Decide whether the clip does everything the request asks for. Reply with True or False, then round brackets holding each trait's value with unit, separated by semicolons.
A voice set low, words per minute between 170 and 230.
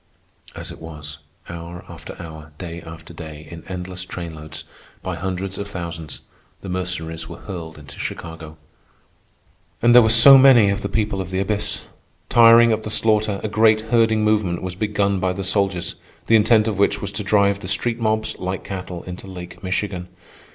True (95 Hz; 180 wpm)